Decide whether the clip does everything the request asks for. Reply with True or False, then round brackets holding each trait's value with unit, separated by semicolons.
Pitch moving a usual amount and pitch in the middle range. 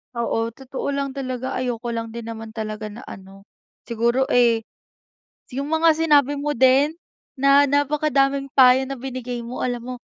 False (3.0 semitones; 255 Hz)